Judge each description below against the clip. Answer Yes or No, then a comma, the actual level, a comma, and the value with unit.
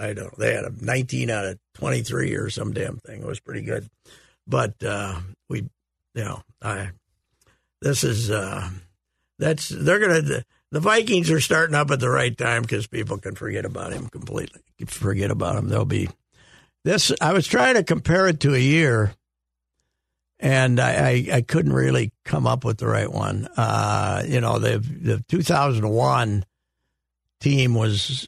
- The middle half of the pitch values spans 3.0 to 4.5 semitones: No, average, 5.2 semitones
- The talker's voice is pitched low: Yes, low, 115 Hz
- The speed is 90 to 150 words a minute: No, average, 175 wpm